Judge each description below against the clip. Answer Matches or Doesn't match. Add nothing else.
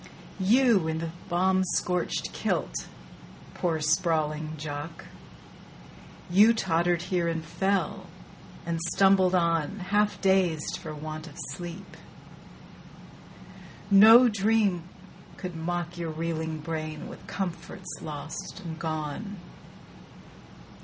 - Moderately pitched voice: Matches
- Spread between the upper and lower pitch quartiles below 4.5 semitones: Matches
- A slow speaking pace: Matches